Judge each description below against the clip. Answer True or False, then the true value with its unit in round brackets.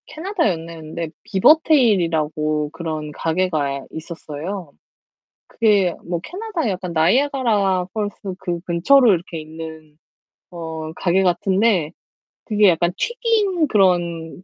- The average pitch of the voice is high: False (180 Hz)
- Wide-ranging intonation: False (5.0 semitones)